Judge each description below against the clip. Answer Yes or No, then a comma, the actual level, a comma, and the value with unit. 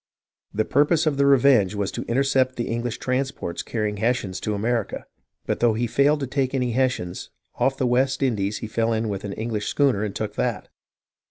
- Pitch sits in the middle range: No, low, 120 Hz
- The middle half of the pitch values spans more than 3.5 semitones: Yes, average, 3.9 semitones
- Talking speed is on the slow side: No, average, 195 wpm